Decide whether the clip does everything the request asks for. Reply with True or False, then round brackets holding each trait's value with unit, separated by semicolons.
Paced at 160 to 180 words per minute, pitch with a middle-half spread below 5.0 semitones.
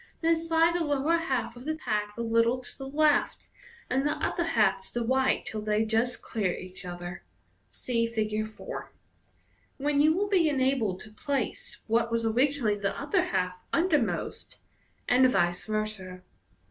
False (170 wpm; 5.4 semitones)